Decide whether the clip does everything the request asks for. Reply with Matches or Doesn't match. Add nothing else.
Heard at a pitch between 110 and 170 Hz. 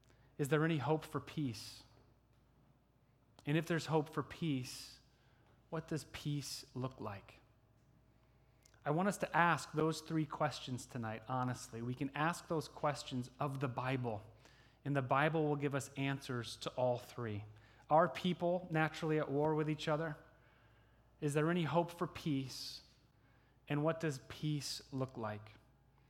Matches